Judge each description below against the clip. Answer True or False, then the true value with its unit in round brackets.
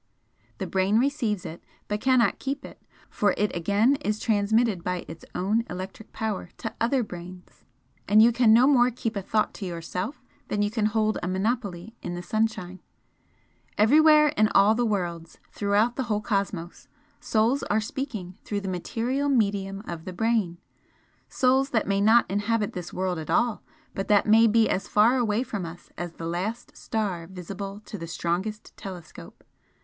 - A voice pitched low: False (210 Hz)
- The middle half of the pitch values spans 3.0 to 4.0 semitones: True (3.7 semitones)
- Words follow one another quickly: False (170 wpm)